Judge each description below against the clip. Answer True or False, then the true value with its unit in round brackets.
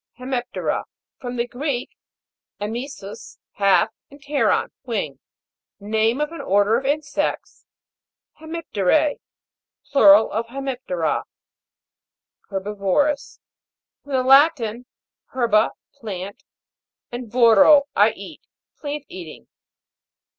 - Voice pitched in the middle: False (240 Hz)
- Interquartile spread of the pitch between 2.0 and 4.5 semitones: False (5.3 semitones)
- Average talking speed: False (95 wpm)